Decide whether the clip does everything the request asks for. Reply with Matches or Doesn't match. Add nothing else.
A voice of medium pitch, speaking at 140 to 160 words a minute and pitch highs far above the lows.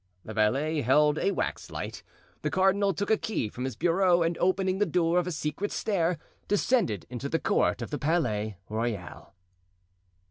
Doesn't match